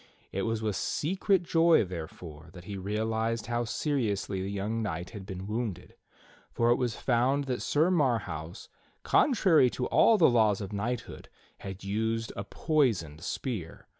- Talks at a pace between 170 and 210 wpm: No, average, 155 wpm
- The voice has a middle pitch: No, low, 110 Hz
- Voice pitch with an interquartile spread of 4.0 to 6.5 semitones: Yes, average, 4.5 semitones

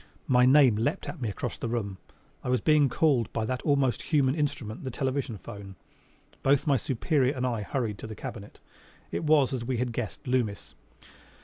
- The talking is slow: No, average, 190 wpm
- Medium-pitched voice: No, low, 125 Hz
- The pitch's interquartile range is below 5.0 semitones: Yes, average, 3.6 semitones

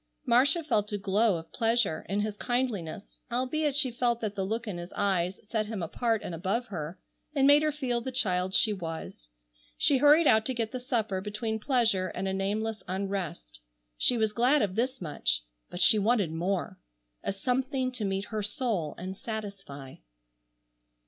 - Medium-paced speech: Yes, average, 180 wpm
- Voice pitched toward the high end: Yes, high, 215 Hz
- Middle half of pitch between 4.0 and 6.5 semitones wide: Yes, average, 4.5 semitones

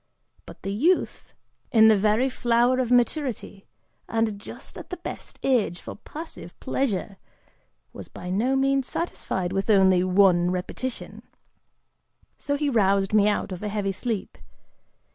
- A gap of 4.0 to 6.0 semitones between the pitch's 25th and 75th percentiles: Yes, average, 4.9 semitones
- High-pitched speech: Yes, high, 215 Hz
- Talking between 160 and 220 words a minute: No, average, 145 wpm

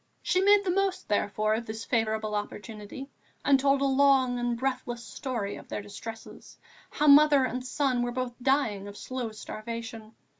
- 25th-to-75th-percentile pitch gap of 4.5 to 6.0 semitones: No, average, 3.9 semitones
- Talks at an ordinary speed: Yes, average, 165 wpm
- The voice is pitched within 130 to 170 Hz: No, high, 245 Hz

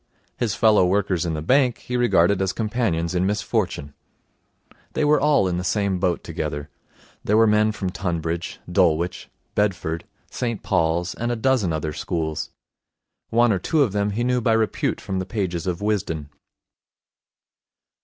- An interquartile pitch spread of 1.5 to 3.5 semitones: No, average, 4.7 semitones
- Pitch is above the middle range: No, very low, 95 Hz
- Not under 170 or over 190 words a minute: No, average, 160 wpm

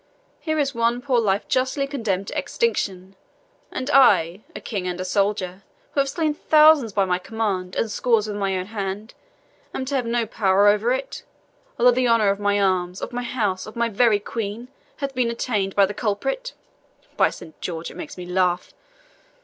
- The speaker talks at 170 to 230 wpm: Yes, average, 190 wpm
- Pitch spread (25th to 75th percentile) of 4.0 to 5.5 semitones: Yes, average, 4.6 semitones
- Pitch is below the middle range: No, high, 215 Hz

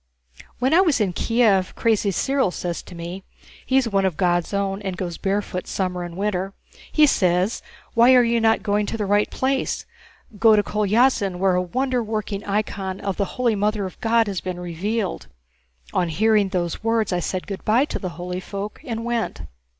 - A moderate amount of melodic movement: Yes, average, 3.6 semitones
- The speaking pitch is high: Yes, high, 205 Hz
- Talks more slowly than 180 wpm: No, average, 190 wpm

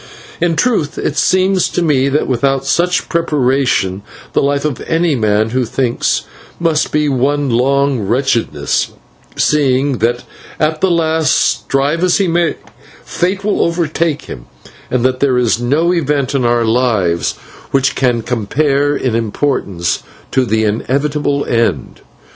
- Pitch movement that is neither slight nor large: Yes, average, 4.3 semitones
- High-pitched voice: No, medium, 140 Hz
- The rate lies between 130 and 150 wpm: Yes, average, 140 wpm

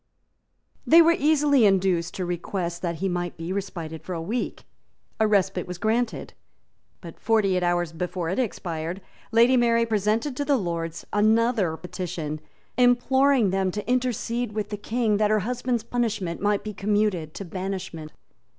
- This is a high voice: Yes, high, 200 Hz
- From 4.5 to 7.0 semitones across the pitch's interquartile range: Yes, average, 4.9 semitones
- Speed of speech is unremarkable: Yes, average, 160 wpm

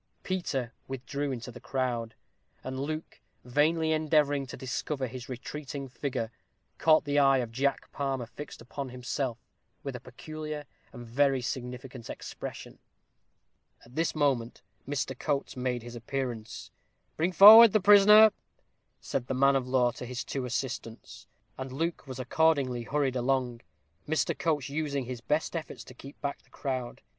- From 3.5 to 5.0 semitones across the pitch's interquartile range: No, average, 3.0 semitones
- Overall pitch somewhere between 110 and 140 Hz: Yes, low, 135 Hz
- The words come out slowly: No, average, 150 wpm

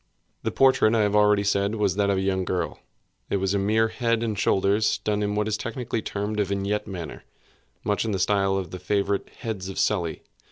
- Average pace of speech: No, fast, 215 wpm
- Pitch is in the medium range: No, low, 100 Hz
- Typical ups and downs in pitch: No, narrow, 1.7 semitones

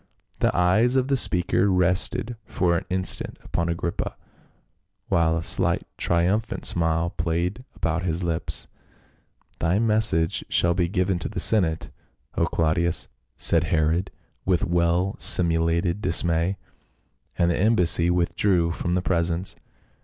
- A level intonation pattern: Yes, narrow, 1.9 semitones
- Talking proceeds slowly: Yes, slow, 130 wpm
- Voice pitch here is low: Yes, very low, 85 Hz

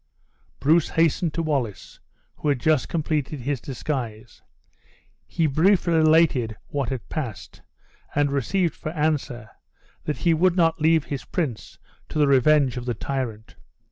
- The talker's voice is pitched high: No, medium, 145 Hz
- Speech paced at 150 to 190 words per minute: No, average, 140 wpm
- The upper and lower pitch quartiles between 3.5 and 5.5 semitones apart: Yes, average, 4.1 semitones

